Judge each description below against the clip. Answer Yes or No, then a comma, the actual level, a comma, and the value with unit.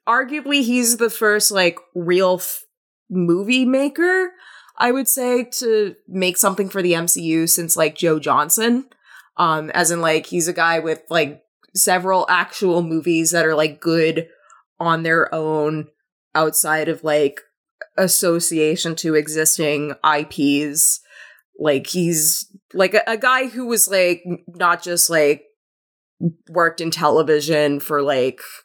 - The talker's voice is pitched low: No, medium, 170 Hz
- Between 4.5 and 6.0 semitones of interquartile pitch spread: Yes, average, 4.8 semitones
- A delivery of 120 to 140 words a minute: Yes, slow, 135 wpm